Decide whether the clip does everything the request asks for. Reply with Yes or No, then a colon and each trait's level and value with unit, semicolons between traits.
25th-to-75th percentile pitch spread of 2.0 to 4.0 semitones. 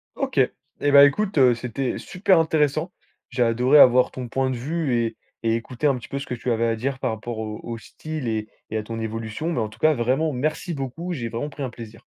No: average, 4.4 semitones